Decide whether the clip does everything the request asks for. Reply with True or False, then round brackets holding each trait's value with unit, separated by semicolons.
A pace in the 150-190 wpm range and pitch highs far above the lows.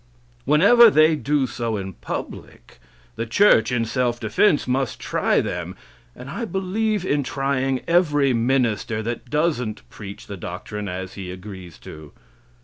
False (140 wpm; 6.2 semitones)